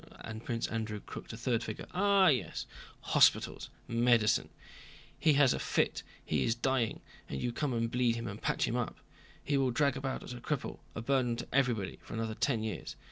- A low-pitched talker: Yes, low, 120 Hz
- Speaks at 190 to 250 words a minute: Yes, average, 195 wpm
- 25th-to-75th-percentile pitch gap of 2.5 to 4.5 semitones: Yes, average, 2.9 semitones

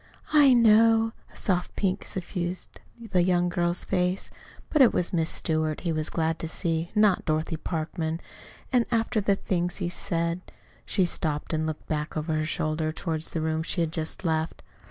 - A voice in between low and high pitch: Yes, medium, 170 Hz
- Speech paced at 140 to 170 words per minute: No, average, 180 wpm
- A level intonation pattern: No, average, 3.1 semitones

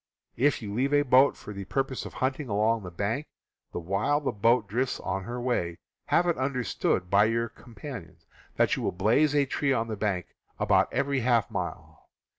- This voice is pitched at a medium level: No, low, 115 Hz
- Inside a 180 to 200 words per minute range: Yes, average, 195 wpm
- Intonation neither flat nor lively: Yes, average, 4.8 semitones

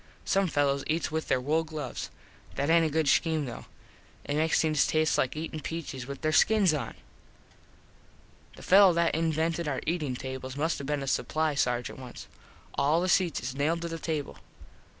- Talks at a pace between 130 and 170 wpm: No, average, 185 wpm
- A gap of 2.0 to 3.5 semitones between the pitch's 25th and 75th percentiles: Yes, average, 2.8 semitones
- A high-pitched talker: No, medium, 155 Hz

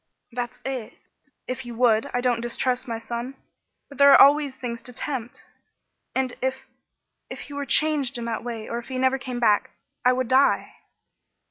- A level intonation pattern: Yes, narrow, 2.0 semitones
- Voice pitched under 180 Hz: No, very high, 250 Hz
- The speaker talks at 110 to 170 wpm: No, average, 180 wpm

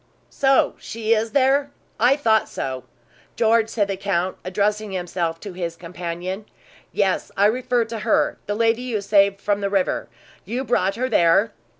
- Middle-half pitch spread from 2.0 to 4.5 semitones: Yes, average, 3.6 semitones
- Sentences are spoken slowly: No, average, 165 wpm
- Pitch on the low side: No, high, 205 Hz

